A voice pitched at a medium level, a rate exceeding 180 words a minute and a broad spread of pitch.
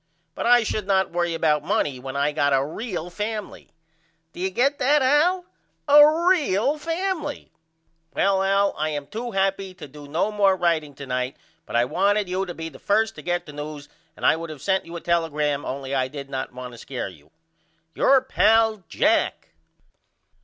Yes: medium, 180 Hz; average, 190 wpm; wide, 7.2 semitones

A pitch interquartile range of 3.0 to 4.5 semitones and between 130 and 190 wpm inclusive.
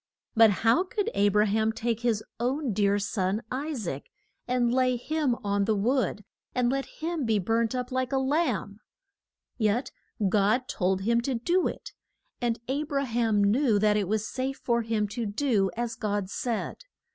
Yes: average, 3.7 semitones; average, 180 wpm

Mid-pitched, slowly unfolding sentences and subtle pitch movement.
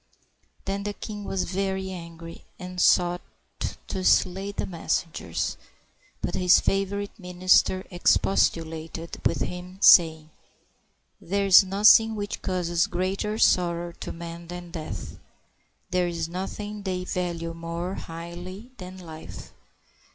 Yes: medium, 180 Hz; slow, 120 wpm; narrow, 2.3 semitones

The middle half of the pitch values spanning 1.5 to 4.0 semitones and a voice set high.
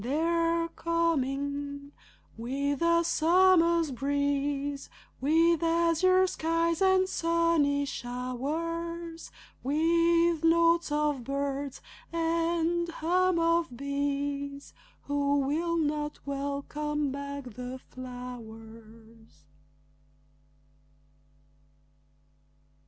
Yes: average, 3.2 semitones; very high, 295 Hz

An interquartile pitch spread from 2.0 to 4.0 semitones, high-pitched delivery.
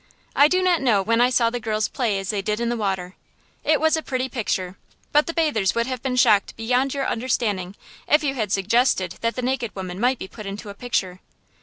No: average, 4.5 semitones; high, 235 Hz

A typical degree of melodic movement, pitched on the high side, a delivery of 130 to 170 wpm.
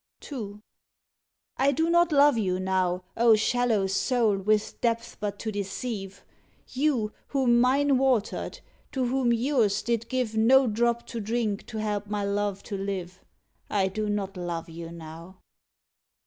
Yes: average, 3.9 semitones; high, 215 Hz; average, 150 wpm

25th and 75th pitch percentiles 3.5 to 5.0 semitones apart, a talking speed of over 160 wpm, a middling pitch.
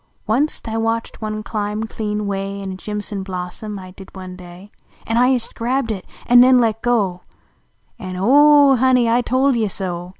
No: average, 4.0 semitones; average, 195 wpm; high, 215 Hz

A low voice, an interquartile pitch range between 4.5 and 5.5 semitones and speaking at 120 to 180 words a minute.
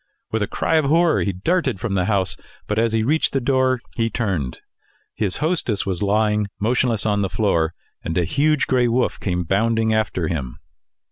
No: low, 110 Hz; average, 4.8 semitones; average, 190 wpm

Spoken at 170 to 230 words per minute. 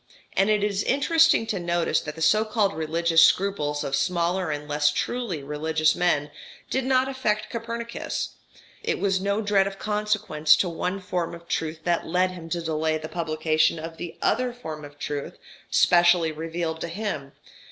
Yes: average, 175 wpm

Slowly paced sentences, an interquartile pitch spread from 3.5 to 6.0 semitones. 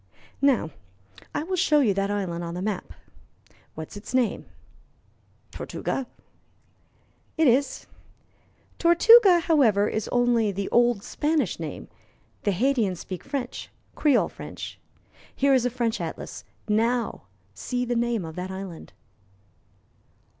Yes: slow, 125 wpm; wide, 5.6 semitones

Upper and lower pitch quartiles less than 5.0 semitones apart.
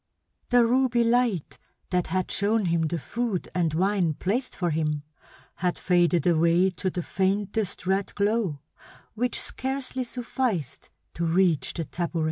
No: average, 5.3 semitones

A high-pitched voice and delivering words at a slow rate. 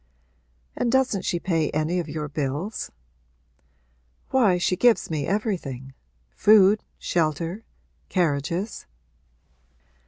No: medium, 175 Hz; slow, 95 wpm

